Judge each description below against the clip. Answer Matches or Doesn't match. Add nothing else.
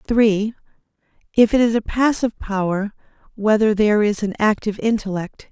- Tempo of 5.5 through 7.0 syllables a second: Matches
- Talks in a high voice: Matches